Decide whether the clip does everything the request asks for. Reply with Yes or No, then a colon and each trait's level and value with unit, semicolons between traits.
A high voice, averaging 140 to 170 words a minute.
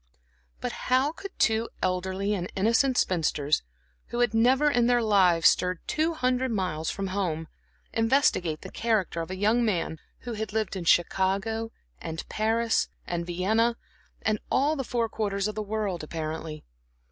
Yes: high, 210 Hz; average, 160 wpm